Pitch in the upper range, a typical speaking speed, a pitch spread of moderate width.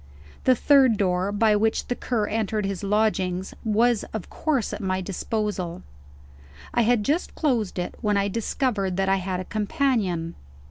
Yes: high, 210 Hz; average, 165 wpm; average, 3.3 semitones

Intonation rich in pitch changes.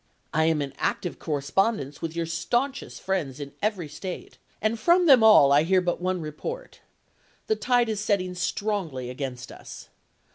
Yes: wide, 6.4 semitones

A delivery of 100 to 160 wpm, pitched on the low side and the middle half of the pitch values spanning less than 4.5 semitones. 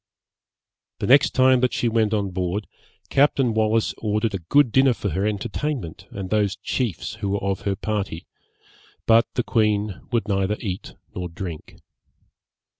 Yes: average, 155 wpm; low, 105 Hz; average, 3.0 semitones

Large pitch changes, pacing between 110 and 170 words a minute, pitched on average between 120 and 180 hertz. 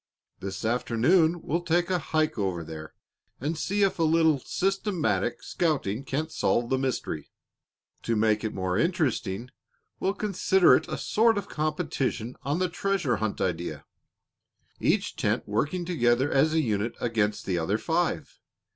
Yes: wide, 7.9 semitones; average, 150 wpm; medium, 140 Hz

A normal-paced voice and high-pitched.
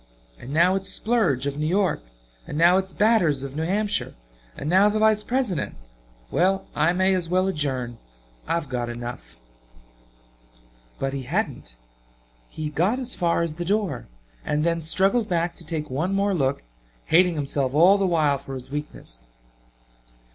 No: average, 160 wpm; medium, 170 Hz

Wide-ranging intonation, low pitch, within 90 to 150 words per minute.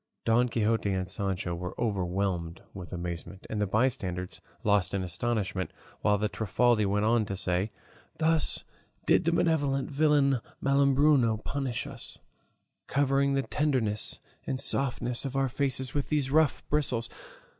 Yes: wide, 5.8 semitones; low, 115 Hz; average, 140 wpm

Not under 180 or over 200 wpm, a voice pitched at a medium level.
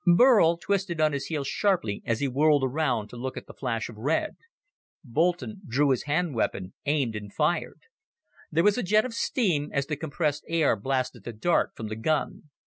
Yes: average, 195 wpm; medium, 145 Hz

